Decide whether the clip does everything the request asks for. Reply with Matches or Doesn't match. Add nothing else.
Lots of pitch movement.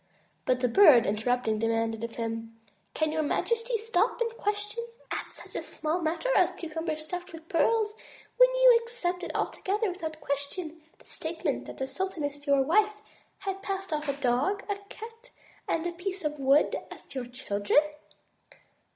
Matches